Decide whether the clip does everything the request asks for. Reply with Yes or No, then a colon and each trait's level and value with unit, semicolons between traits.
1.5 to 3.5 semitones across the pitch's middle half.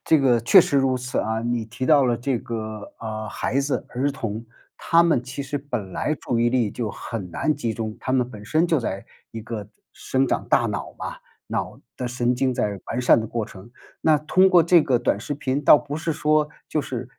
No: average, 4.2 semitones